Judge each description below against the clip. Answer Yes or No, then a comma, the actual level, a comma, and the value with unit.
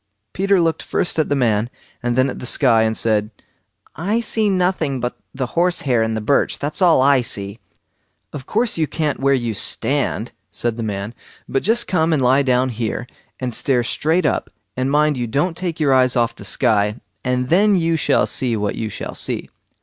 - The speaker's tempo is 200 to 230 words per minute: Yes, fast, 205 wpm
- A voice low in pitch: Yes, low, 130 Hz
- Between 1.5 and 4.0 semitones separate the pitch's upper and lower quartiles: No, wide, 5.6 semitones